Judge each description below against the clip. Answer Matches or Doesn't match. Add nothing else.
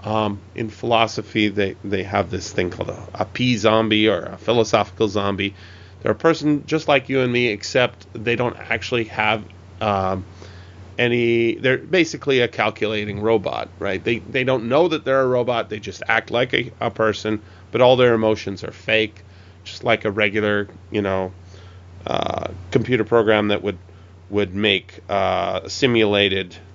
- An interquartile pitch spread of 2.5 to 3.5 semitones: Matches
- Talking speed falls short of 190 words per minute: Matches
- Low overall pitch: Matches